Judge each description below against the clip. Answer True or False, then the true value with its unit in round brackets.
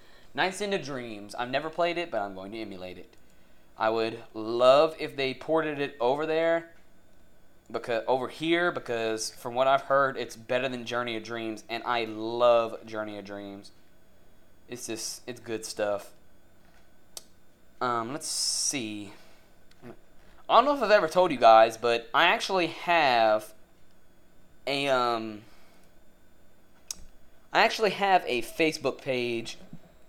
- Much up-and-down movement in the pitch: True (5.7 semitones)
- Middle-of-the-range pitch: False (120 Hz)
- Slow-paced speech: False (145 wpm)